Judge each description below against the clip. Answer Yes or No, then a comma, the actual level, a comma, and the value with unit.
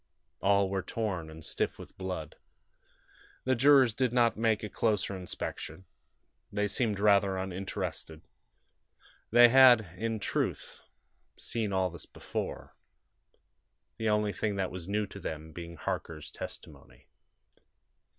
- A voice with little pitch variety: No, average, 3.4 semitones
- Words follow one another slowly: Yes, slow, 125 wpm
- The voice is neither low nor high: No, low, 100 Hz